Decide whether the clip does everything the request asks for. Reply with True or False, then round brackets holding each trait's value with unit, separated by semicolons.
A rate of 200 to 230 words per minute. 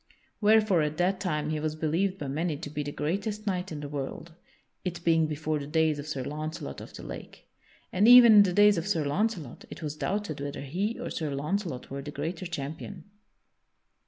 True (205 wpm)